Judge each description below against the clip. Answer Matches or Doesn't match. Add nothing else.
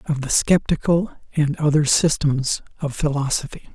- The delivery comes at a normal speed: Doesn't match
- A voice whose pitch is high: Doesn't match